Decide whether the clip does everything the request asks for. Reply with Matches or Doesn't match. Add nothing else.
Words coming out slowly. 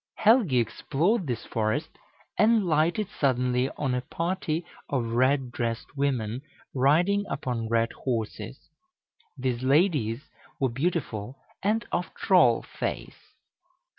Matches